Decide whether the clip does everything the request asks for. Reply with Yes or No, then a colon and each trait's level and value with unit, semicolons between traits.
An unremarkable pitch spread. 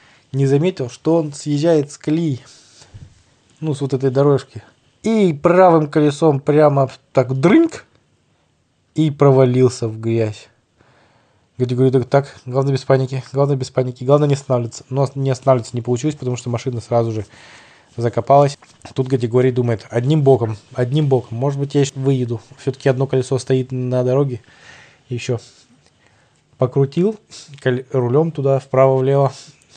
No: narrow, 2.2 semitones